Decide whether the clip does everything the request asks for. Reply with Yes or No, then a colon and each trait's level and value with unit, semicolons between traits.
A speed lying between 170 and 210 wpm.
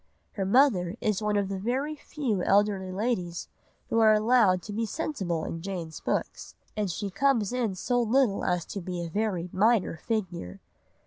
Yes: average, 175 wpm